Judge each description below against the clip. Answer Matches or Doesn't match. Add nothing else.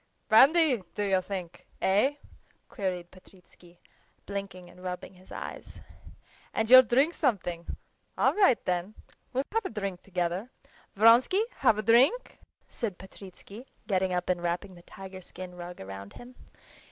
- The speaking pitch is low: Doesn't match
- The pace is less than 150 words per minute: Matches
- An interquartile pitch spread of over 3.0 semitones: Matches